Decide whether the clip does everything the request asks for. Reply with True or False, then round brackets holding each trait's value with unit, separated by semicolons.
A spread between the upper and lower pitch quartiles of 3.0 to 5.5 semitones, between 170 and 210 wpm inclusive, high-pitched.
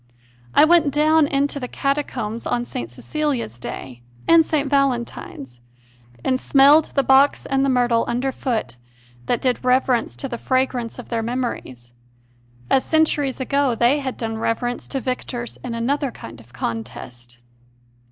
False (3.3 semitones; 150 wpm; 255 Hz)